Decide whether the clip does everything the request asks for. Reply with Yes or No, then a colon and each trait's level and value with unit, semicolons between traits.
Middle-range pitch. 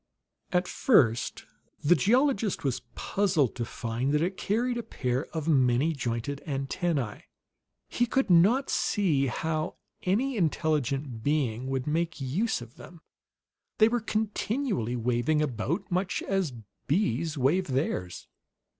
Yes: medium, 155 Hz